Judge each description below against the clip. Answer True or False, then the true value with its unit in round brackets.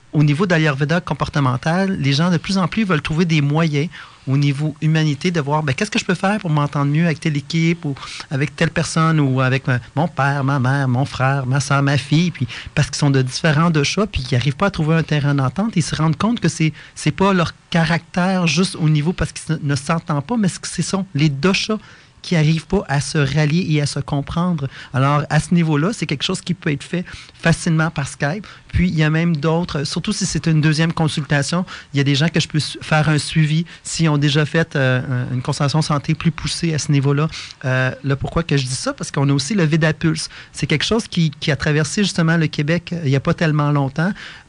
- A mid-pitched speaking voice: True (155 Hz)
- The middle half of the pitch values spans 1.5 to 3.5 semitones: True (2.9 semitones)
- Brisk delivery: True (245 wpm)